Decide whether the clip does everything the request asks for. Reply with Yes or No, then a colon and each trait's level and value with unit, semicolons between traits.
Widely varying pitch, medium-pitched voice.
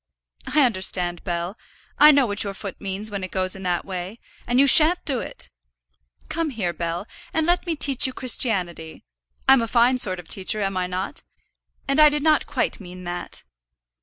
No: wide, 6.8 semitones; high, 205 Hz